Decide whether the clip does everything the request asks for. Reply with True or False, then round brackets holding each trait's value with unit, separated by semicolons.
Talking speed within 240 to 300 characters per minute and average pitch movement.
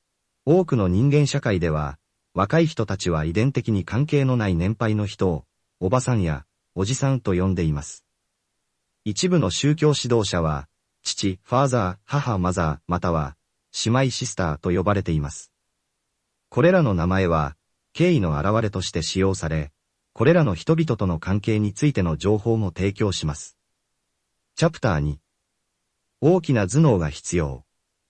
False (290 characters per minute; 6.7 semitones)